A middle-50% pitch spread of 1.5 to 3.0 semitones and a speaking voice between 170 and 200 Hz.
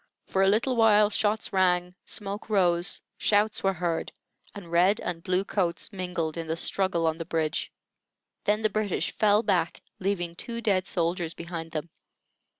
No: average, 3.4 semitones; medium, 185 Hz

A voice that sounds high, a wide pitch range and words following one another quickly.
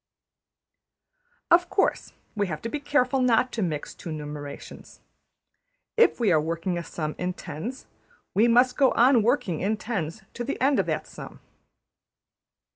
No: high, 220 Hz; wide, 7.2 semitones; average, 155 wpm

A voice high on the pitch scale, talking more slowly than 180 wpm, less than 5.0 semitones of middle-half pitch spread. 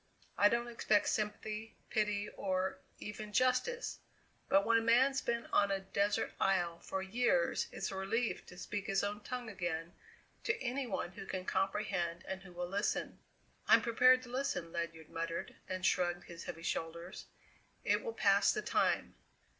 Yes: high, 200 Hz; average, 165 wpm; average, 4.6 semitones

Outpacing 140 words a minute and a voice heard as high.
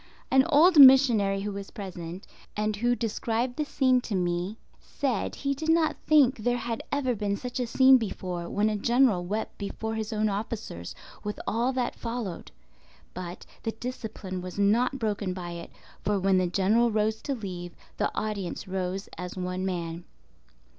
Yes: average, 170 wpm; high, 215 Hz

